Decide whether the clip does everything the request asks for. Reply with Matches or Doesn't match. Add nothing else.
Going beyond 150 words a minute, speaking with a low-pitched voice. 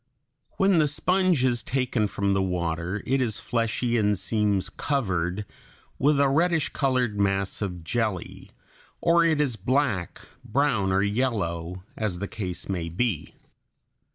Doesn't match